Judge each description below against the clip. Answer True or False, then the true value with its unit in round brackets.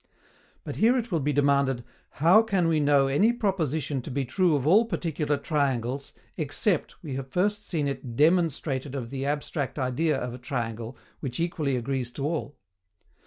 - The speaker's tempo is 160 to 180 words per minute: True (170 wpm)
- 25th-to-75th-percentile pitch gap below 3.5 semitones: False (4.0 semitones)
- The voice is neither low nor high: True (145 Hz)